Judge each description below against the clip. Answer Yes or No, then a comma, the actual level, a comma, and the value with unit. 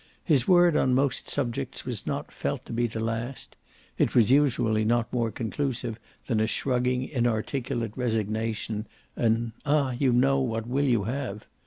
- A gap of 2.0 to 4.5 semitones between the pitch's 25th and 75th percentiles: Yes, average, 2.9 semitones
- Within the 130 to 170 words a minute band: Yes, average, 160 wpm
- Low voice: Yes, low, 120 Hz